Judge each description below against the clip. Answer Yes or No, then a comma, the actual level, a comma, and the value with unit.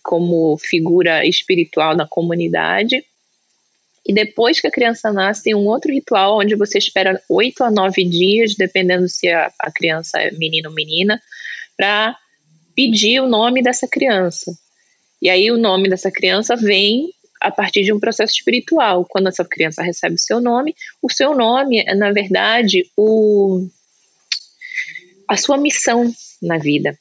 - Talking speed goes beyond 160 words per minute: No, average, 150 wpm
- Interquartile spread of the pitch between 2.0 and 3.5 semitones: No, average, 4.8 semitones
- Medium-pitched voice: No, high, 205 Hz